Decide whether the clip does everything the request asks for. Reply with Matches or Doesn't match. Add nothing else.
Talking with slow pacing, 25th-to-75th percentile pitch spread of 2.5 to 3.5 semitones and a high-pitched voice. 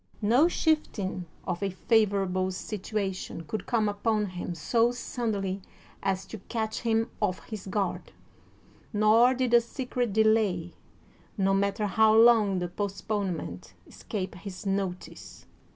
Matches